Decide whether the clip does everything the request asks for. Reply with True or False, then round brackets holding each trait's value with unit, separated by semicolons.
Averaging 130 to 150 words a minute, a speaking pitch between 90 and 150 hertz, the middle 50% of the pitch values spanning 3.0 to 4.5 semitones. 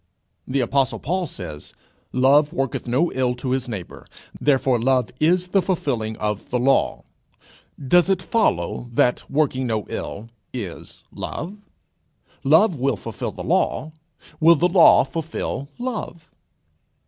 False (135 wpm; 135 Hz; 5.5 semitones)